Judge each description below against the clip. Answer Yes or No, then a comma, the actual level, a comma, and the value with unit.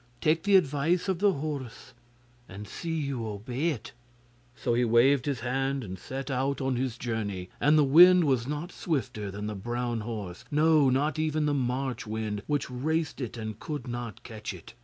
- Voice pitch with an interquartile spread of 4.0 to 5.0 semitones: Yes, average, 4.6 semitones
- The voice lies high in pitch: No, low, 130 Hz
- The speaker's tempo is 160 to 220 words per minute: Yes, average, 185 wpm